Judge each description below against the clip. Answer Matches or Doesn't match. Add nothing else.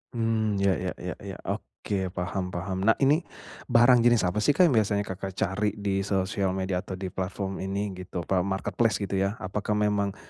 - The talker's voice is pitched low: Matches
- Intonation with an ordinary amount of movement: Doesn't match